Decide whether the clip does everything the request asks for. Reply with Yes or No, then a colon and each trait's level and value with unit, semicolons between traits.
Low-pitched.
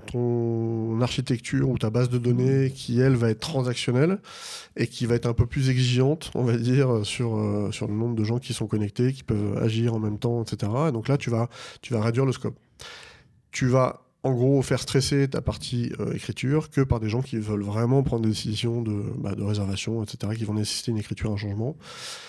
Yes: low, 120 Hz